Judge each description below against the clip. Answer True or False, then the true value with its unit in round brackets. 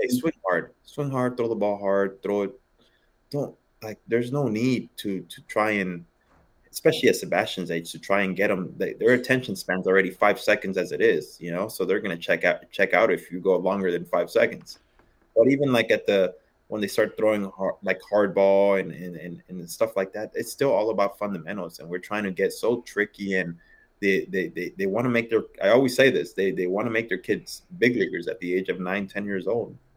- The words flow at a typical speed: False (230 wpm)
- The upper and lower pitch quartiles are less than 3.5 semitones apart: False (4.1 semitones)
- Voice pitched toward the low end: True (100 Hz)